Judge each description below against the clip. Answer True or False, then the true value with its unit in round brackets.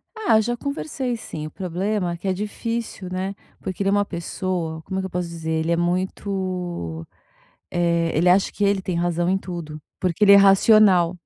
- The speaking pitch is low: False (185 Hz)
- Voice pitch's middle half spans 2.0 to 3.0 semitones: True (2.7 semitones)